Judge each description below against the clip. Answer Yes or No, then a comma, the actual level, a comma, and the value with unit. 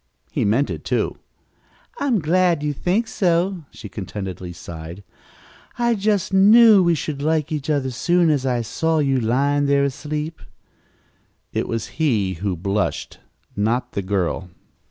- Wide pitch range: Yes, wide, 8.3 semitones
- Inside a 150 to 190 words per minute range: Yes, average, 155 wpm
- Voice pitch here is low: No, medium, 145 Hz